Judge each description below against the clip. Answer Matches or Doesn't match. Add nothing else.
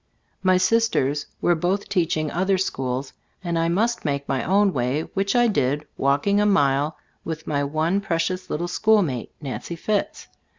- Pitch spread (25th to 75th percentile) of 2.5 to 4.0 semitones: Doesn't match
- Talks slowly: Doesn't match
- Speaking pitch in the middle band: Matches